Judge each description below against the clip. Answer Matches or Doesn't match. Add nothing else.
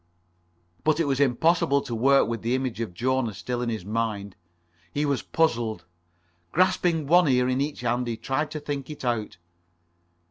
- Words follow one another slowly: Doesn't match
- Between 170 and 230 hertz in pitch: Doesn't match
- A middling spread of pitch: Matches